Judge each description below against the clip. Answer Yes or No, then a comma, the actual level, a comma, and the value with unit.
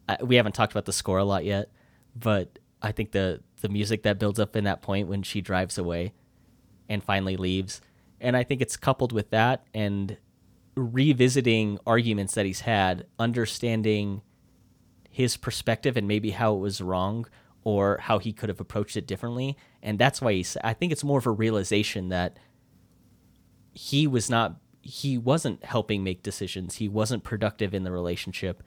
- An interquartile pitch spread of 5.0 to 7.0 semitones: No, average, 3.3 semitones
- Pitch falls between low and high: No, low, 105 Hz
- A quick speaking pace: No, average, 175 wpm